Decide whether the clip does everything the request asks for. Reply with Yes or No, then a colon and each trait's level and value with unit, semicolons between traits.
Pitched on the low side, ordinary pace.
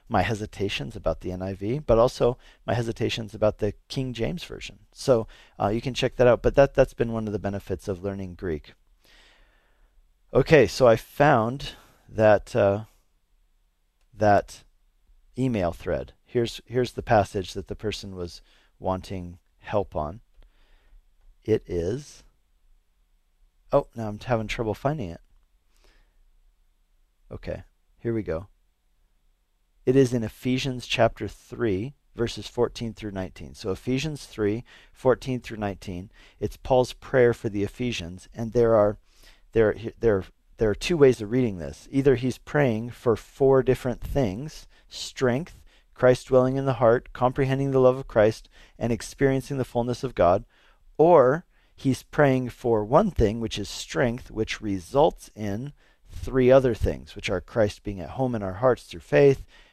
Yes: low, 110 Hz; average, 150 wpm